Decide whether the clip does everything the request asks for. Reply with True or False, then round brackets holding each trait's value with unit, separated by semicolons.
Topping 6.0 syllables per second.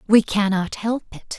False (4.2 syllables/s)